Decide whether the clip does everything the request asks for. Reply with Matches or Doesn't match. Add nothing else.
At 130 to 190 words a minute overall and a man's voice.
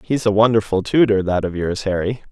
Doesn't match